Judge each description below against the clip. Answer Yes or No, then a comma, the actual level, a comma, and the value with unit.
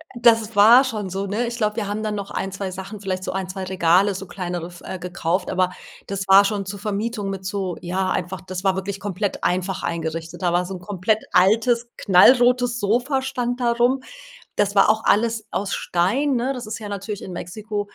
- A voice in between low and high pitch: No, high, 200 Hz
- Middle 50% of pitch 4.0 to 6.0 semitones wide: No, average, 3.1 semitones